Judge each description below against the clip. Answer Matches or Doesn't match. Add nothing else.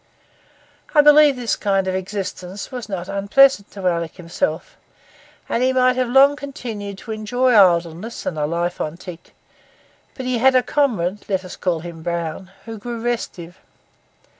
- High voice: Matches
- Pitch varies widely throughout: Matches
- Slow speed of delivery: Doesn't match